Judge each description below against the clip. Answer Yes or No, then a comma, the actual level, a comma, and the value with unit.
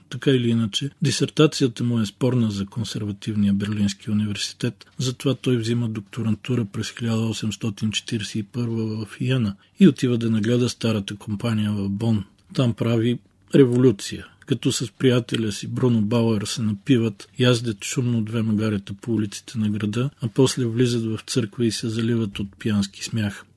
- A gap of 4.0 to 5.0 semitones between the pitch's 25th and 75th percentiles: No, average, 2.8 semitones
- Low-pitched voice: Yes, low, 115 Hz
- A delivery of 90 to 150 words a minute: Yes, average, 145 wpm